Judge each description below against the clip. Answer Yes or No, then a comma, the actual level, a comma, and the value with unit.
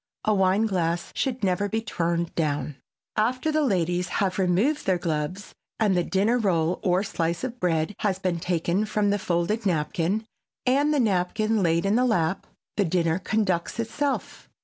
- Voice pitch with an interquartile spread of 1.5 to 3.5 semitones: No, average, 4.2 semitones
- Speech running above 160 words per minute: Yes, average, 170 wpm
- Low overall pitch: No, high, 190 Hz